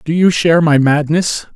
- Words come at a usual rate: Yes, average, 195 wpm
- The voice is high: No, medium, 160 Hz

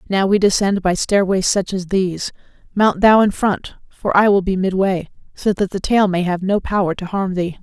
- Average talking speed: No, fast, 220 wpm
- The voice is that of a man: No, female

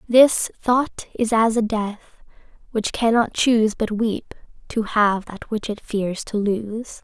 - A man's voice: No, female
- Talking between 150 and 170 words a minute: Yes, average, 160 wpm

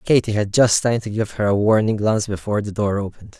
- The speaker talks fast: Yes, fast, 250 wpm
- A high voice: No, low, 105 Hz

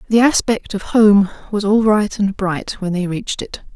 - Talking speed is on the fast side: Yes, fast, 210 wpm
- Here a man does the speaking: No, female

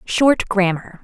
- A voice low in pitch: No, high, 200 Hz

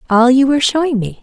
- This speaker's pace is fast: Yes, fast, 245 wpm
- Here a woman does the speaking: Yes, female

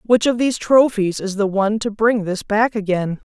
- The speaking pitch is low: No, high, 215 Hz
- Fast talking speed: Yes, fast, 220 wpm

